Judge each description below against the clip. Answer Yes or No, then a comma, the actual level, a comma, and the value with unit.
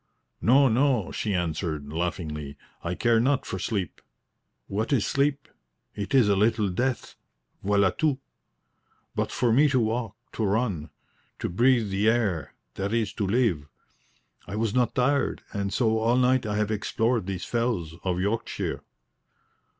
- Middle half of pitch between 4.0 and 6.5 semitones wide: Yes, average, 4.3 semitones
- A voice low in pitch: Yes, low, 110 Hz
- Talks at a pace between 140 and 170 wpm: Yes, average, 150 wpm